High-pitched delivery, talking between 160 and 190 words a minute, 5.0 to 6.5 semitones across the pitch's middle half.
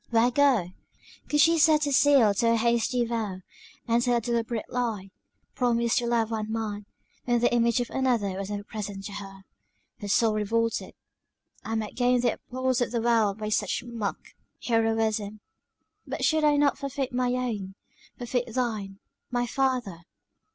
No: high, 235 Hz; average, 165 wpm; average, 2.7 semitones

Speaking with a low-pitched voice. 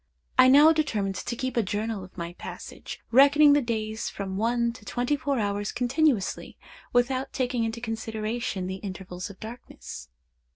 No: high, 230 Hz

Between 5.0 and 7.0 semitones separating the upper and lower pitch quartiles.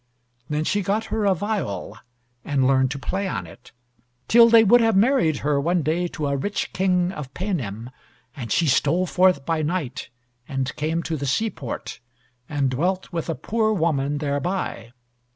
Yes: wide, 5.5 semitones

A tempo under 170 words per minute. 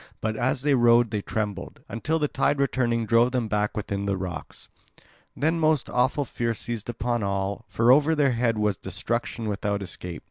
No: average, 180 wpm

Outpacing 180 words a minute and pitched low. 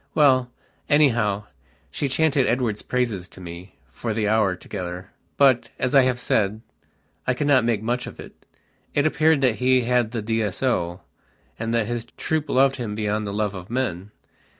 No: average, 175 wpm; low, 115 Hz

